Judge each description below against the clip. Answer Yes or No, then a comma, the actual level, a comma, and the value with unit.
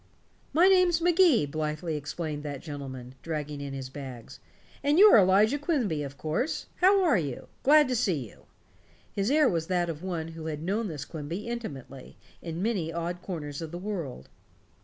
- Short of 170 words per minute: No, average, 175 wpm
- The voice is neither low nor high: Yes, medium, 165 Hz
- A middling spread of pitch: No, wide, 8.0 semitones